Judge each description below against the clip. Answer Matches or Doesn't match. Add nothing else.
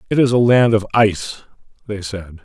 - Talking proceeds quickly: Doesn't match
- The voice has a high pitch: Doesn't match